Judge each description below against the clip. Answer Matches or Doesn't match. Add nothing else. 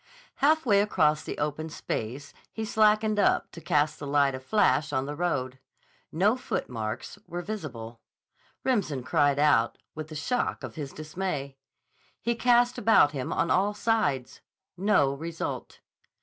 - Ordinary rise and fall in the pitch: Doesn't match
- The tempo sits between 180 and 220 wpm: Doesn't match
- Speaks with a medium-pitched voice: Matches